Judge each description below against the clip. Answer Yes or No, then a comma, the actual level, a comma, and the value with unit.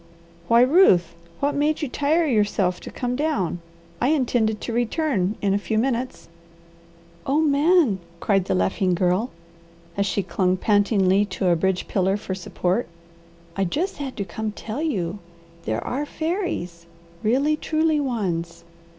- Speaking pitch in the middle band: No, high, 220 Hz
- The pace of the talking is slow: No, average, 150 wpm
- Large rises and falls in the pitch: Yes, wide, 7.2 semitones